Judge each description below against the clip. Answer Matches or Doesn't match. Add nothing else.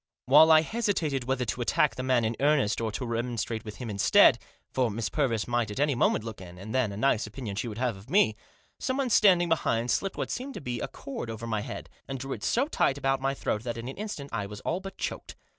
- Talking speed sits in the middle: Doesn't match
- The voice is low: Matches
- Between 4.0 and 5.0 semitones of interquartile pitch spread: Matches